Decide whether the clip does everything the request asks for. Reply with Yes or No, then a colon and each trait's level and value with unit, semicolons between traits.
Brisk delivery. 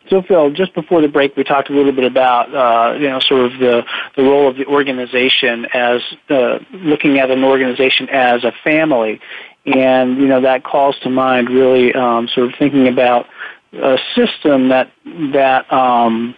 No: average, 185 wpm